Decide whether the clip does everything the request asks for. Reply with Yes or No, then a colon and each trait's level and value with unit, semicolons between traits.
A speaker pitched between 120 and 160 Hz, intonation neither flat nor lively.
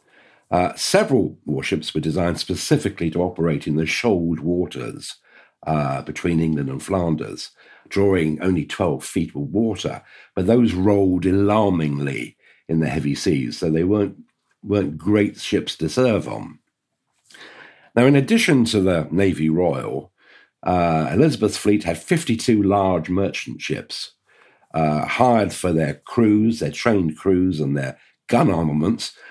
No: very low, 90 Hz; average, 4.7 semitones